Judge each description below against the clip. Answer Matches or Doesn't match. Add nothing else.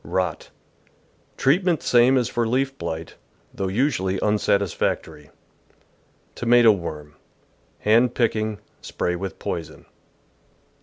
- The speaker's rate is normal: Doesn't match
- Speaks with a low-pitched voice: Matches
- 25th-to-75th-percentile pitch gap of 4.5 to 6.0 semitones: Matches